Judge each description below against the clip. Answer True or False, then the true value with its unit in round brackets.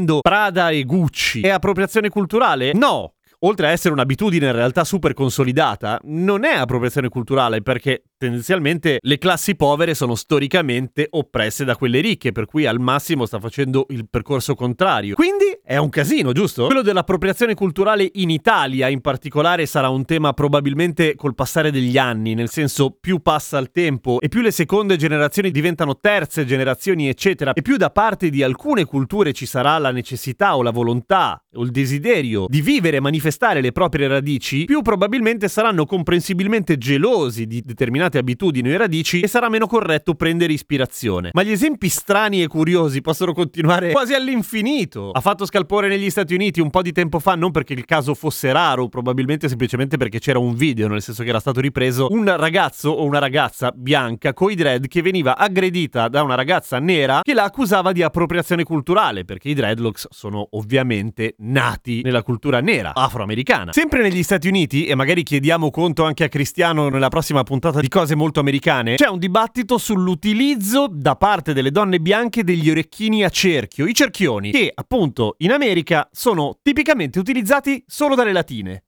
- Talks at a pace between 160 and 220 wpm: True (170 wpm)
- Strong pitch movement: True (6.2 semitones)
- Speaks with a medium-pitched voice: True (155 Hz)